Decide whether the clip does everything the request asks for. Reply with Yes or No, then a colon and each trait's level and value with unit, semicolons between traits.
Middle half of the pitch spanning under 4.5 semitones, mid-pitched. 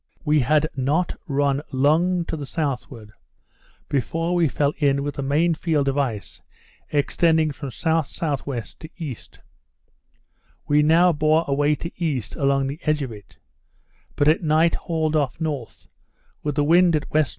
Yes: narrow, 2.6 semitones; medium, 150 Hz